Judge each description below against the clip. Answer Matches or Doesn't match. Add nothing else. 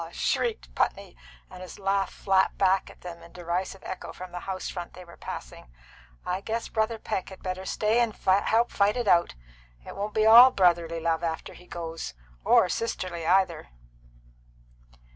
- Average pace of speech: Matches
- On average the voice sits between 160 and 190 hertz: Matches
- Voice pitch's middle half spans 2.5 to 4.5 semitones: Matches